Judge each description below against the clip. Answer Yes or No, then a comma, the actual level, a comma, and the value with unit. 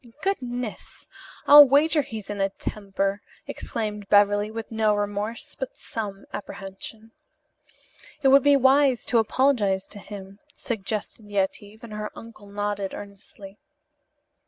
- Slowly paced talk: Yes, slow, 125 wpm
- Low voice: No, high, 210 Hz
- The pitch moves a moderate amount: Yes, average, 3.2 semitones